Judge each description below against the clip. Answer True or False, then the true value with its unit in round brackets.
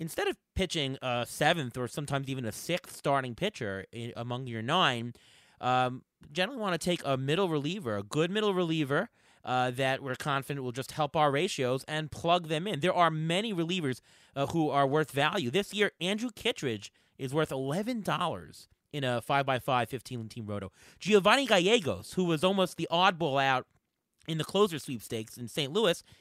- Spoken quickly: False (185 wpm)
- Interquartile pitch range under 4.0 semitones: False (5.6 semitones)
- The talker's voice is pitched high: False (145 Hz)